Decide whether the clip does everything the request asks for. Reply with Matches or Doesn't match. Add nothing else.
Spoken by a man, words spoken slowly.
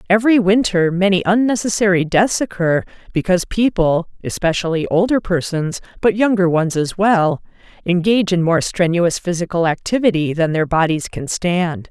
Doesn't match